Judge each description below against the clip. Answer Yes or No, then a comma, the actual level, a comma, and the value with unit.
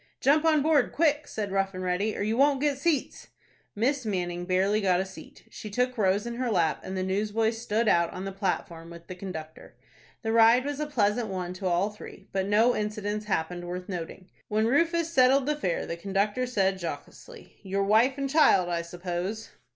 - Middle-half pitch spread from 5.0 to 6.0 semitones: Yes, average, 5.3 semitones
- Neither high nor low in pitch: No, high, 205 Hz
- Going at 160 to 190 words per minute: No, average, 200 wpm